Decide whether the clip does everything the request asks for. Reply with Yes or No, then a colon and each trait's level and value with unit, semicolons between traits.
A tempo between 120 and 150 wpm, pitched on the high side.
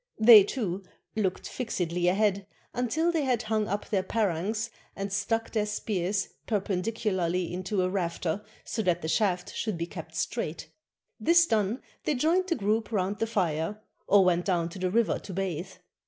No: average, 170 wpm; high, 200 Hz